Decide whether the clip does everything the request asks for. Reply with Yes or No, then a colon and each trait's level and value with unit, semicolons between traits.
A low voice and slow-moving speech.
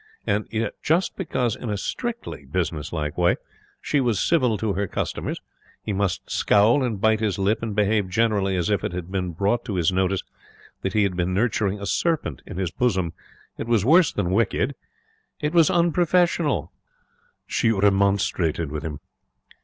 No: low, 100 Hz; average, 175 wpm